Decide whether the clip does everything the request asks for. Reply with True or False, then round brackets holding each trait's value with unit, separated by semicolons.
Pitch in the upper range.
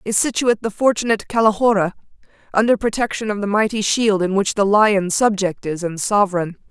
True (205 Hz)